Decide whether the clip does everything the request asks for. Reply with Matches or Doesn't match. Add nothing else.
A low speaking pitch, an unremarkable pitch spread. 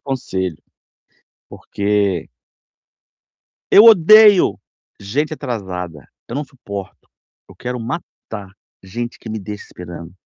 Doesn't match